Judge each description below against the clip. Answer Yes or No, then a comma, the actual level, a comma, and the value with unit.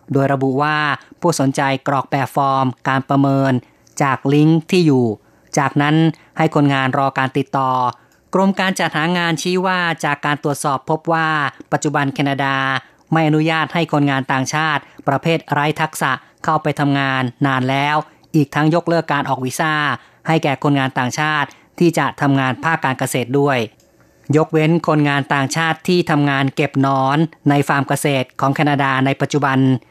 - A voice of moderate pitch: Yes, medium, 145 Hz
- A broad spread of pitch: No, average, 2.7 semitones